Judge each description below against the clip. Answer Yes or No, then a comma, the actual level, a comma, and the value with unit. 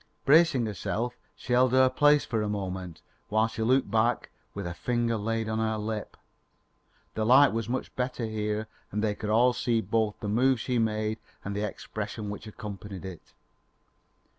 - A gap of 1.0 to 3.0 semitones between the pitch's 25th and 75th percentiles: Yes, narrow, 2.6 semitones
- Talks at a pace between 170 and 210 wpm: Yes, average, 175 wpm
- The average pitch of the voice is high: No, low, 110 Hz